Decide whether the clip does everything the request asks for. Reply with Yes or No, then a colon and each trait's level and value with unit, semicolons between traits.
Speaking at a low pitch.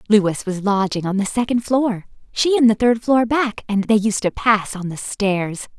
No: high, 215 Hz